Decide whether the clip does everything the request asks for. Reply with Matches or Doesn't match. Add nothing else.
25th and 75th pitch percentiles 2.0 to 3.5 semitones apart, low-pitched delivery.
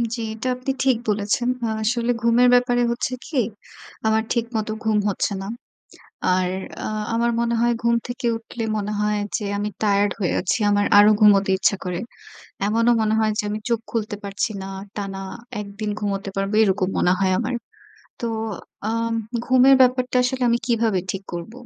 Doesn't match